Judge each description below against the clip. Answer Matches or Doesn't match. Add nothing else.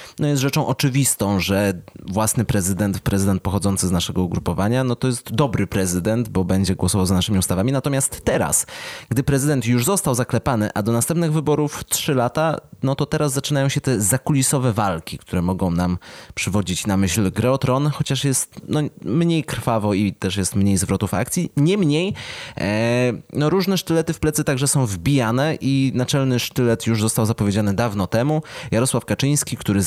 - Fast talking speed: Matches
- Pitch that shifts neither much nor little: Doesn't match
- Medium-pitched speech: Doesn't match